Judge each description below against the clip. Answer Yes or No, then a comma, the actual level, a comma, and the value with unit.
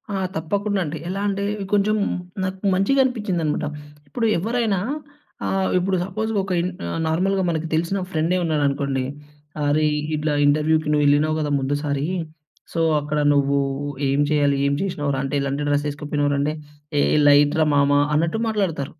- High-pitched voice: No, medium, 155 Hz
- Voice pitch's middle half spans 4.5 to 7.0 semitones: Yes, average, 4.8 semitones